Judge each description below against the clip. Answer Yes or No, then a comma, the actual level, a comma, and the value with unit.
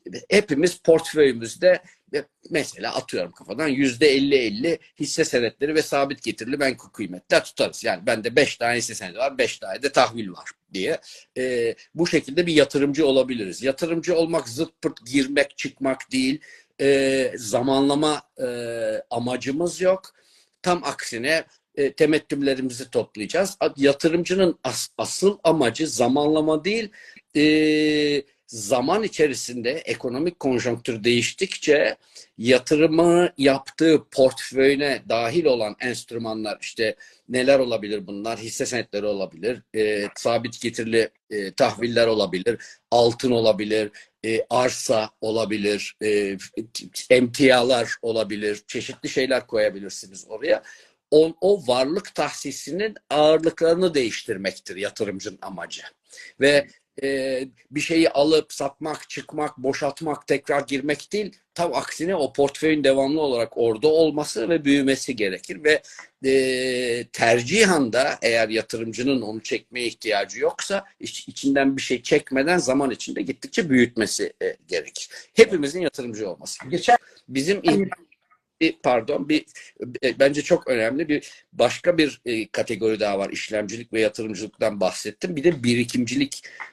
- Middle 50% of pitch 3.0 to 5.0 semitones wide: No, wide, 5.4 semitones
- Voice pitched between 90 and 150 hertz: Yes, medium, 140 Hz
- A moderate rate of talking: Yes, average, 115 wpm